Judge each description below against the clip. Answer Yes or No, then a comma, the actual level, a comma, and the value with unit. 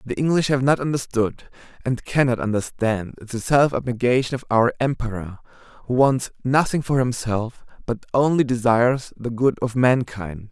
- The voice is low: Yes, low, 125 Hz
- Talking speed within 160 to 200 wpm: No, average, 150 wpm